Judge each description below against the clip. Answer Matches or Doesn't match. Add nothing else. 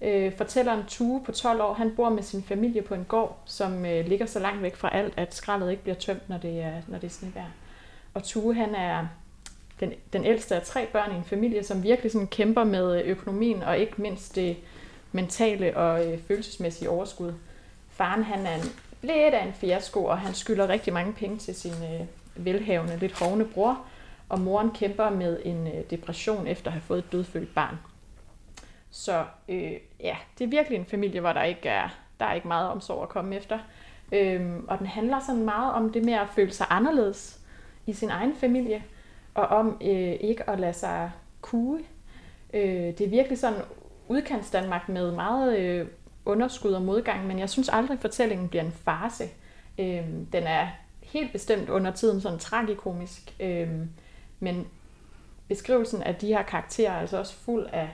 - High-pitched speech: Matches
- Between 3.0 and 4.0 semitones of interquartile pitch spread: Matches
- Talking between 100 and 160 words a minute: Doesn't match